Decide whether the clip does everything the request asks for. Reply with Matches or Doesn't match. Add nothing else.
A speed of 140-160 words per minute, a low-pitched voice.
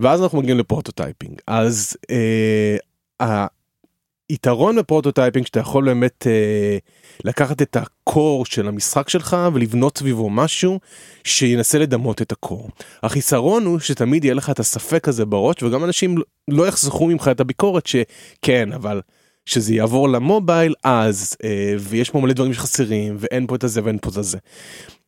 Matches